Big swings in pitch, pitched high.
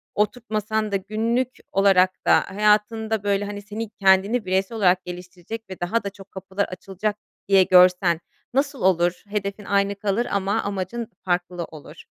No: narrow, 2.4 semitones; high, 200 Hz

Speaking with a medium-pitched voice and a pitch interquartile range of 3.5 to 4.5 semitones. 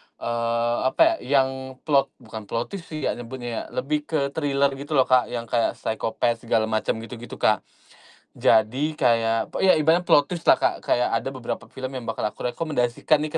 No: low, 125 Hz; average, 3.8 semitones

